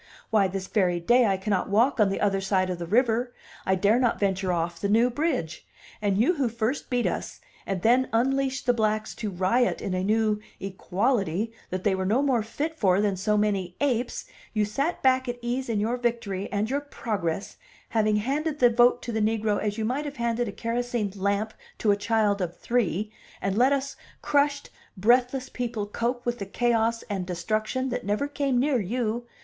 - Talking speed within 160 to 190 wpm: No, average, 200 wpm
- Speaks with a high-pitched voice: Yes, high, 220 Hz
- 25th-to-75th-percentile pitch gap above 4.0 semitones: No, average, 3.7 semitones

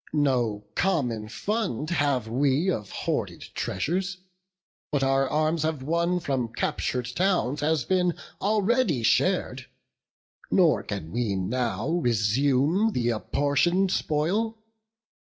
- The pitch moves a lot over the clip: Yes, wide, 6.6 semitones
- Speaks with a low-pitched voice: No, medium, 145 Hz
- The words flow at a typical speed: No, slow, 110 wpm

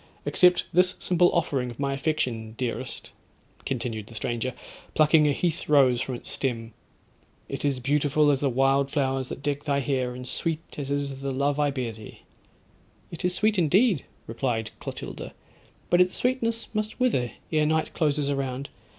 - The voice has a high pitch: No, medium, 140 Hz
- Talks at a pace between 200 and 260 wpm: No, average, 165 wpm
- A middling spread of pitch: Yes, average, 3.7 semitones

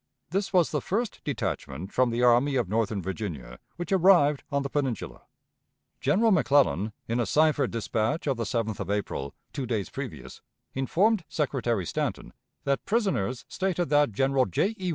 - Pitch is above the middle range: No, low, 135 Hz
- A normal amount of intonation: No, wide, 6.6 semitones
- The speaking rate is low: No, average, 160 wpm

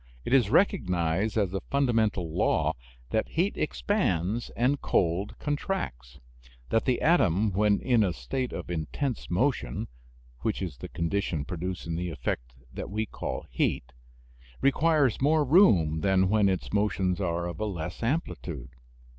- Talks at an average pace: Yes, average, 145 wpm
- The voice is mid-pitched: No, low, 100 Hz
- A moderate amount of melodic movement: No, wide, 6.7 semitones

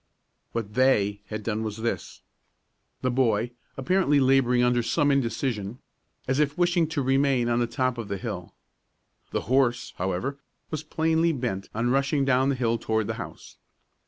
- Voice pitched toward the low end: Yes, low, 125 Hz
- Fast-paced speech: No, average, 165 wpm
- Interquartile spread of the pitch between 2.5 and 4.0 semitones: Yes, average, 3.5 semitones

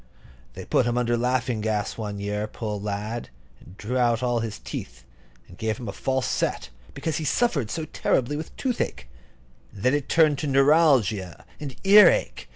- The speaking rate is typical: Yes, average, 175 wpm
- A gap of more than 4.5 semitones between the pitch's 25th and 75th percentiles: Yes, average, 5.3 semitones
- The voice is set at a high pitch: No, low, 120 Hz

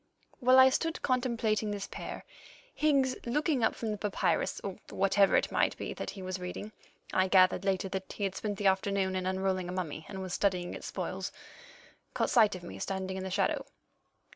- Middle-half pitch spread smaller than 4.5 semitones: Yes, average, 2.9 semitones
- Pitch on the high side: Yes, high, 195 Hz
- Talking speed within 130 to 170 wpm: No, average, 195 wpm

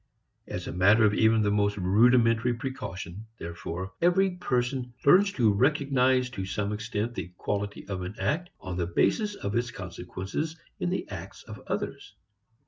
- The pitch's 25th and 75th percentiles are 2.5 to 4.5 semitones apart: No, average, 5.1 semitones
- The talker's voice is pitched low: Yes, low, 110 Hz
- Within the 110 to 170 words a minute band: Yes, average, 160 wpm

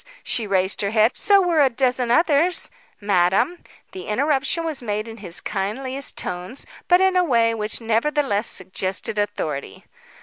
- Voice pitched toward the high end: Yes, high, 230 Hz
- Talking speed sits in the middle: Yes, average, 160 wpm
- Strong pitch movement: Yes, wide, 6.4 semitones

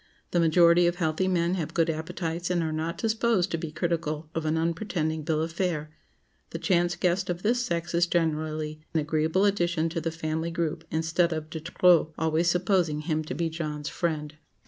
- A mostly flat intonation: Yes, narrow, 1.8 semitones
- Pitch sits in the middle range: Yes, medium, 165 Hz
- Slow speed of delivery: No, average, 190 wpm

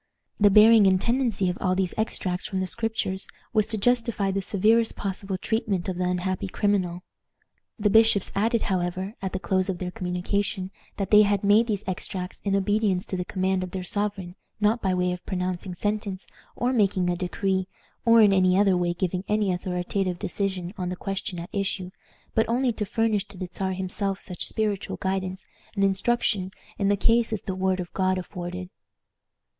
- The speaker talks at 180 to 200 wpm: Yes, average, 185 wpm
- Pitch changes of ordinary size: No, narrow, 2.3 semitones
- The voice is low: No, high, 190 Hz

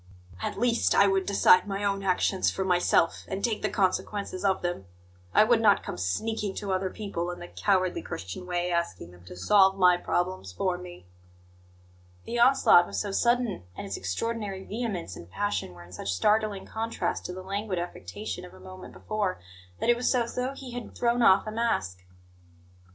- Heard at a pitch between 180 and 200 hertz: Yes, high, 190 Hz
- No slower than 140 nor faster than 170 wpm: No, average, 190 wpm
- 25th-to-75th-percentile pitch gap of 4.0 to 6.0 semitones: No, average, 3.6 semitones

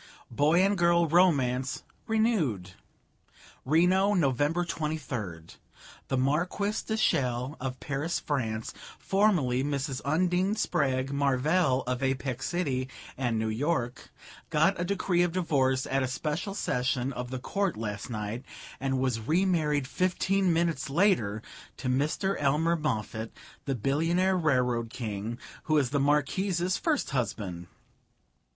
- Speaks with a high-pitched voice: No, medium, 140 Hz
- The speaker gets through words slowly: Yes, slow, 125 wpm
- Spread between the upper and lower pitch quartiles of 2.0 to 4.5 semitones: No, wide, 5.5 semitones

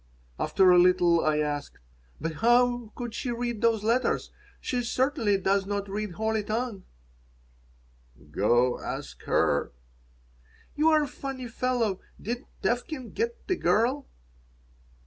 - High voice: Yes, high, 225 Hz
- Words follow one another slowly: Yes, slow, 125 wpm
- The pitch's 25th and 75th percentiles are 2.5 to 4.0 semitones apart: No, average, 4.6 semitones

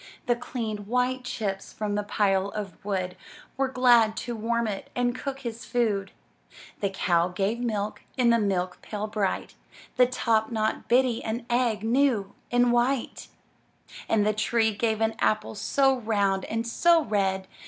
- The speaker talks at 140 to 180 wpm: Yes, average, 160 wpm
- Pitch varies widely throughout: No, average, 3.0 semitones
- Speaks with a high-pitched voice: Yes, high, 220 Hz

